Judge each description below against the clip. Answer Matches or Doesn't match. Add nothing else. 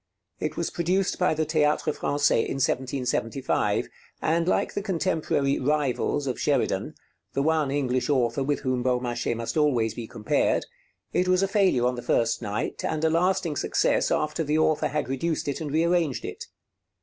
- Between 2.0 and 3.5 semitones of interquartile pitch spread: Doesn't match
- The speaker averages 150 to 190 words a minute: Matches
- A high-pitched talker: Doesn't match